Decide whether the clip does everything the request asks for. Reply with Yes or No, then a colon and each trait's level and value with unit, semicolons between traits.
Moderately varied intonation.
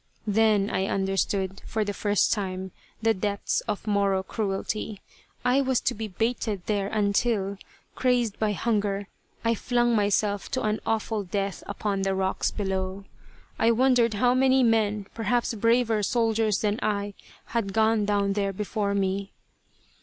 No: narrow, 2.2 semitones